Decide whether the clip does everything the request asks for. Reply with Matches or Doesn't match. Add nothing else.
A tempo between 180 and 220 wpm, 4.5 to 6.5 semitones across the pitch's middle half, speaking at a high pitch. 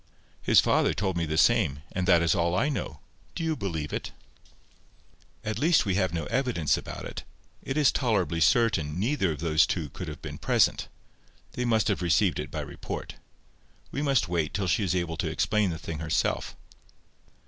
Doesn't match